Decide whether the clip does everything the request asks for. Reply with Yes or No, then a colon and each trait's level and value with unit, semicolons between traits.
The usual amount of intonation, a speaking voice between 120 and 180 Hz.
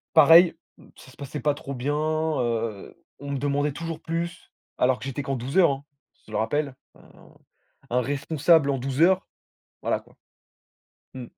Yes: average, 3.4 semitones; medium, 140 Hz